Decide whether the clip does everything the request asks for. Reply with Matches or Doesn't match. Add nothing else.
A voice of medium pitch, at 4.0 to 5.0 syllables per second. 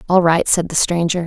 Doesn't match